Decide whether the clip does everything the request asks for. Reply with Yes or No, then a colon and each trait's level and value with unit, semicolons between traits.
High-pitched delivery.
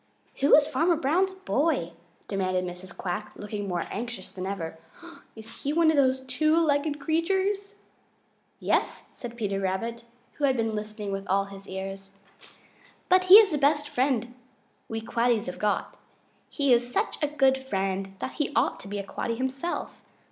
Yes: high, 240 Hz